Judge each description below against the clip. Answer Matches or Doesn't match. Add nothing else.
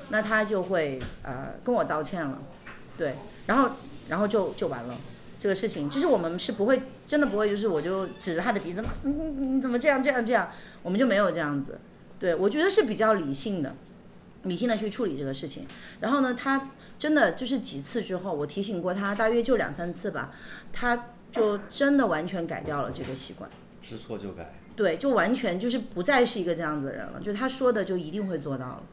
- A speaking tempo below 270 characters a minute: Doesn't match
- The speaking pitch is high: Matches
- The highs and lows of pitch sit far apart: Matches